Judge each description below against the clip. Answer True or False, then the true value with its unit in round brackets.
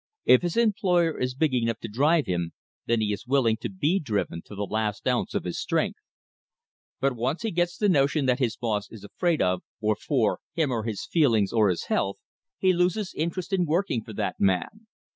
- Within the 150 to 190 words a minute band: False (205 wpm)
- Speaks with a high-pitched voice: False (130 Hz)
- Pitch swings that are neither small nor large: False (8.0 semitones)